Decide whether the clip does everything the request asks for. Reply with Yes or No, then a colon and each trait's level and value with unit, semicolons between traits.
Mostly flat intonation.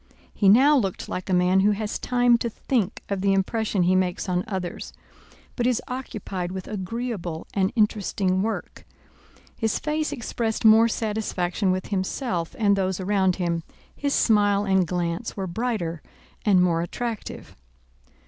No: average, 3.5 semitones